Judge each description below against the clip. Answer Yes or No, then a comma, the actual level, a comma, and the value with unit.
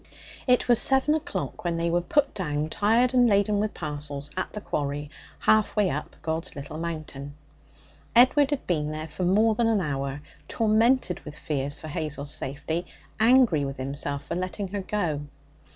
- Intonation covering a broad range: Yes, wide, 6.7 semitones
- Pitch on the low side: No, medium, 170 Hz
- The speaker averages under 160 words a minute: No, average, 170 wpm